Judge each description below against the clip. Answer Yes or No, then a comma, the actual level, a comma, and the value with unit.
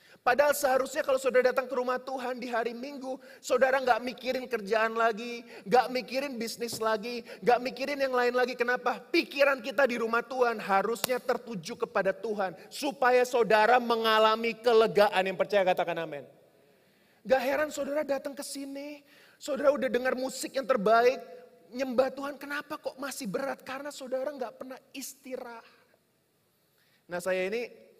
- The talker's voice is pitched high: Yes, very high, 250 Hz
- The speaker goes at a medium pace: No, fast, 150 wpm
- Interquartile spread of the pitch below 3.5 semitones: Yes, average, 2.8 semitones